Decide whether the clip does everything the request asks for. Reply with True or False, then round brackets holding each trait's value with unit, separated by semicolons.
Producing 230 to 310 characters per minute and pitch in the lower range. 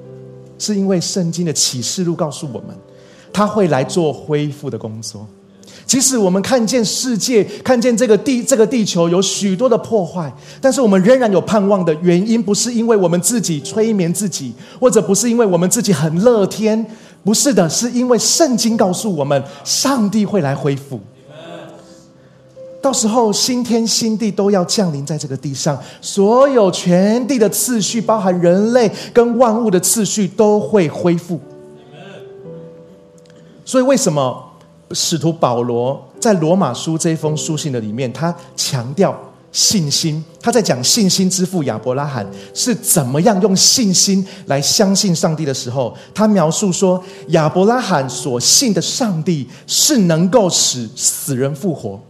False (240 characters per minute; 185 Hz)